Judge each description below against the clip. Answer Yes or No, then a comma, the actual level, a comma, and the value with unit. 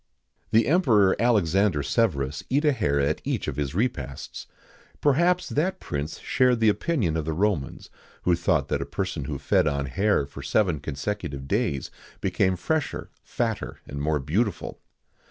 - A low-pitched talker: Yes, very low, 90 Hz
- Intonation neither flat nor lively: No, wide, 8.2 semitones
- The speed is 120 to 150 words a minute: No, average, 160 wpm